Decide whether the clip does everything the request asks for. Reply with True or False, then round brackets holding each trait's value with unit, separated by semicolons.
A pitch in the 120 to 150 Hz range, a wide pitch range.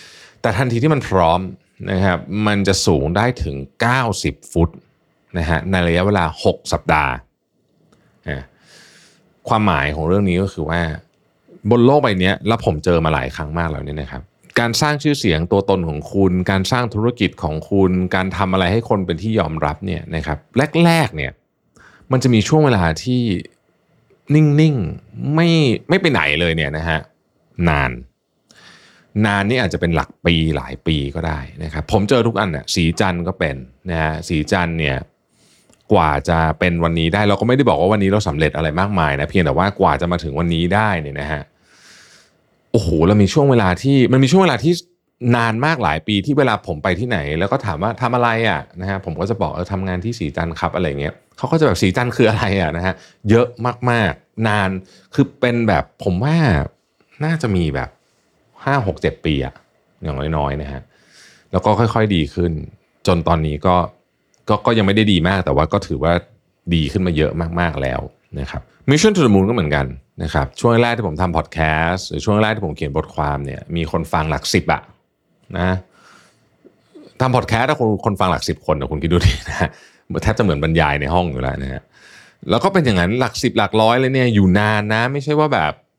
False (95 Hz; 6.0 semitones)